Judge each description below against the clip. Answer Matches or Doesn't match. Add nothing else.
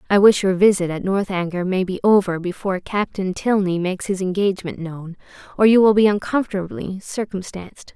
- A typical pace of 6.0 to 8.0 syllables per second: Doesn't match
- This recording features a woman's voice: Matches